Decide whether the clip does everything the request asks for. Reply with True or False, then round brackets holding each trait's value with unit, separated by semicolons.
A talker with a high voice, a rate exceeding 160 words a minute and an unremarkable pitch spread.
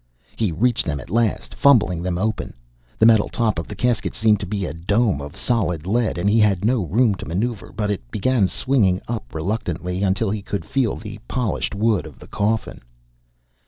False (105 Hz; 195 wpm; 4.1 semitones)